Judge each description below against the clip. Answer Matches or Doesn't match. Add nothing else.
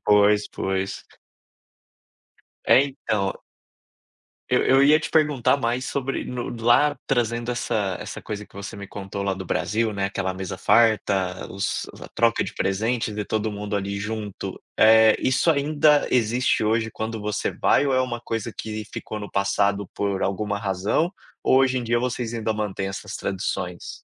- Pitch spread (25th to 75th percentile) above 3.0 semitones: Matches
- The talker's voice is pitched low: Matches